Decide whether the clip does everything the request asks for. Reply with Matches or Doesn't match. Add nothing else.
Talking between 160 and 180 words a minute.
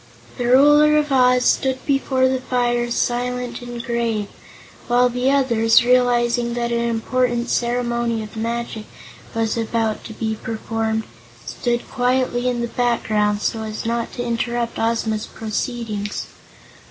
Doesn't match